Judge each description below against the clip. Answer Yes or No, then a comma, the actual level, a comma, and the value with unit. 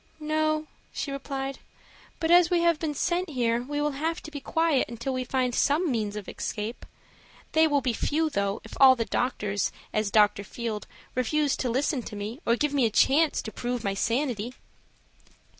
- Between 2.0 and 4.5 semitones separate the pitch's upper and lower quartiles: No, average, 4.9 semitones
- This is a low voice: No, very high, 265 Hz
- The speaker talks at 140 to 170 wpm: No, average, 190 wpm